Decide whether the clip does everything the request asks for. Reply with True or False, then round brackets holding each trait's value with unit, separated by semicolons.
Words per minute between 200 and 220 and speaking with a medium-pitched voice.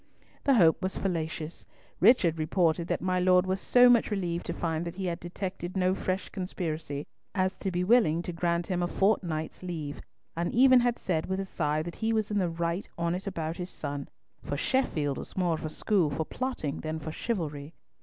True (205 wpm; 175 Hz)